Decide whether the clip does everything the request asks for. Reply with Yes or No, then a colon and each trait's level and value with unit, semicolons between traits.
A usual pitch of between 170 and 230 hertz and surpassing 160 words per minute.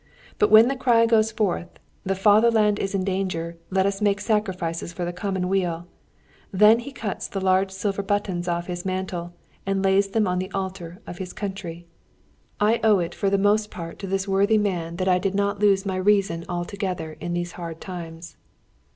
Yes: high, 190 Hz; average, 190 wpm